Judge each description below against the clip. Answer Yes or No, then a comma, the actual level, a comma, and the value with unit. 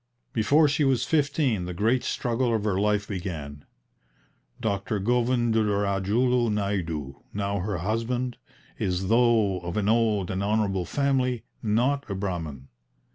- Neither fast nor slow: No, slow, 130 wpm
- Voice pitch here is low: Yes, low, 105 Hz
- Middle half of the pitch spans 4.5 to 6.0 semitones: No, average, 4.0 semitones